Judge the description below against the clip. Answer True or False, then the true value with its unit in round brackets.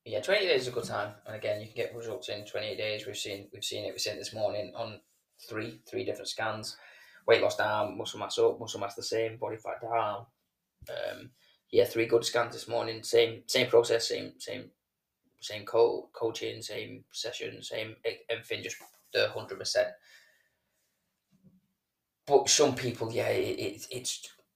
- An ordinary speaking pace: True (180 wpm)